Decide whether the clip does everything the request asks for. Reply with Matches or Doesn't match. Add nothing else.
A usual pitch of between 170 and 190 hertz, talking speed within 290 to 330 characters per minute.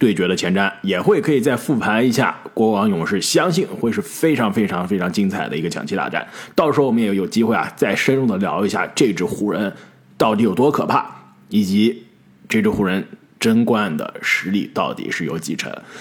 Doesn't match